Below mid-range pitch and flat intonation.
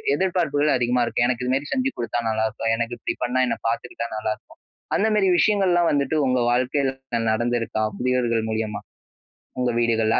No: low, 125 Hz; average, 3.8 semitones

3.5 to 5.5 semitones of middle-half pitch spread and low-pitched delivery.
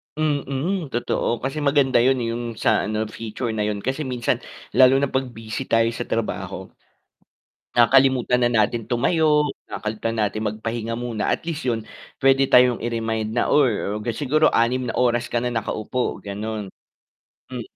No: average, 3.0 semitones; low, 120 Hz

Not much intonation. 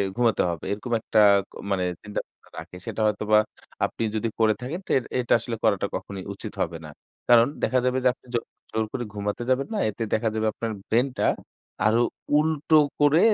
No: average, 3.1 semitones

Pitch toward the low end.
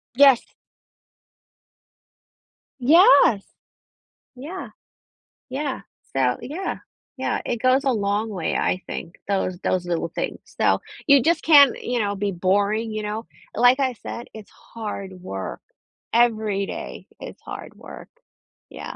No: high, 220 Hz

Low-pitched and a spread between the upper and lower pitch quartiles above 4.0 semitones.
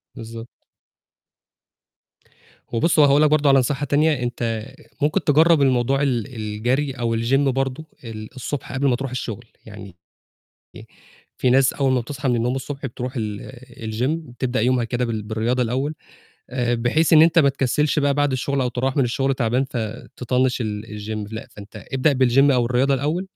No: low, 130 Hz; average, 3.2 semitones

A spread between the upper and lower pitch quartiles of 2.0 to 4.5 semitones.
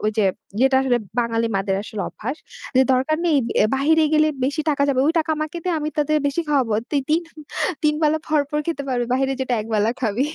Yes: average, 4.1 semitones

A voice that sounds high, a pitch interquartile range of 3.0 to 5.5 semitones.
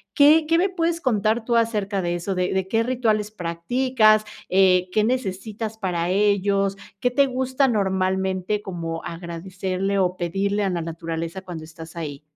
Yes: high, 195 Hz; average, 3.9 semitones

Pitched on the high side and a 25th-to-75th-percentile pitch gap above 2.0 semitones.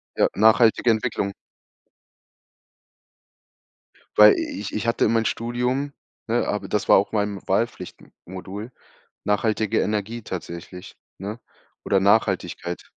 No: low, 105 Hz; narrow, 2.6 semitones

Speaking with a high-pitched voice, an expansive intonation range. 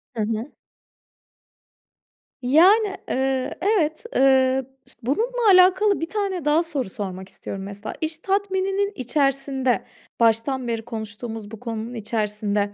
Yes: very high, 265 Hz; wide, 8.3 semitones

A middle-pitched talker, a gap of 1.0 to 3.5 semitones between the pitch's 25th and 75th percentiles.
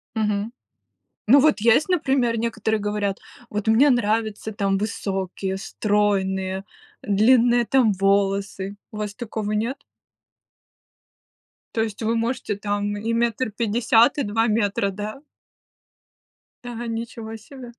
No: high, 215 Hz; narrow, 2.4 semitones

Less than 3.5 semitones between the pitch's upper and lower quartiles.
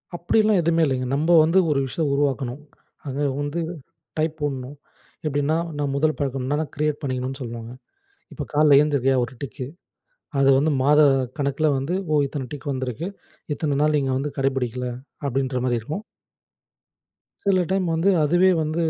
Yes: average, 2.8 semitones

